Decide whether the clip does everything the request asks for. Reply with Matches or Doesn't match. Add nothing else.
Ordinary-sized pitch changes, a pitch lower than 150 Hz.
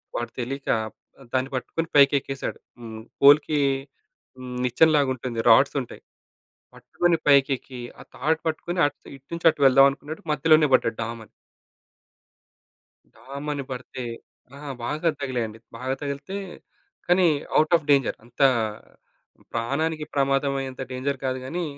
Matches